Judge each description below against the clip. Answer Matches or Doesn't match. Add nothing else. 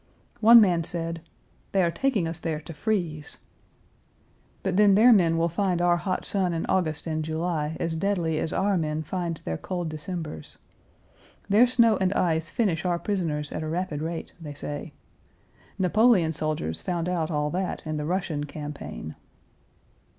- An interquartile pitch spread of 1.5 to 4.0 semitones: Matches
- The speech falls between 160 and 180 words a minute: Matches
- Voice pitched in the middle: Matches